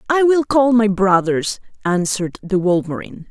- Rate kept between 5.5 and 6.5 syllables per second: No, 5.0 syllables/s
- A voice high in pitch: Yes, high, 205 Hz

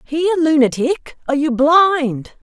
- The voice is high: Yes, very high, 295 Hz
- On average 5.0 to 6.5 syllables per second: No, 4.4 syllables/s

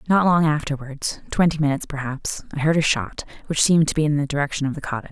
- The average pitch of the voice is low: No, medium, 150 Hz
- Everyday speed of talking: No, fast, 210 wpm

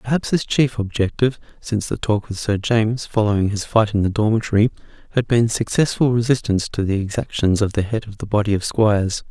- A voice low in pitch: Yes, low, 110 Hz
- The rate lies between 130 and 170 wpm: No, average, 200 wpm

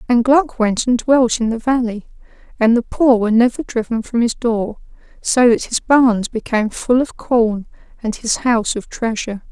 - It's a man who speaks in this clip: No, female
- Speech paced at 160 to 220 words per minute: Yes, average, 190 wpm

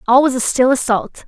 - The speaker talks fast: Yes, fast, 285 wpm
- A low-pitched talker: No, very high, 255 Hz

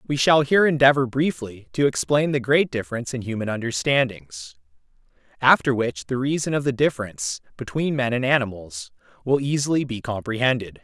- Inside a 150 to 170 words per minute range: Yes, average, 155 wpm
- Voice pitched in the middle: No, low, 125 Hz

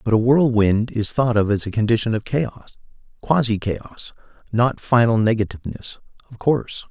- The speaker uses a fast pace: No, average, 150 wpm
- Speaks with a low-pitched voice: Yes, low, 115 Hz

